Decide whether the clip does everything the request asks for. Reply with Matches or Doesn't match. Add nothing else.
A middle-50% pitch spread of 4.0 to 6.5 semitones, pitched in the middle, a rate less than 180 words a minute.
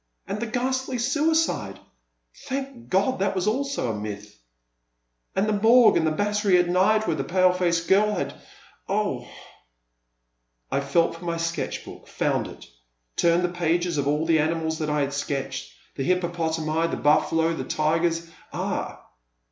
Matches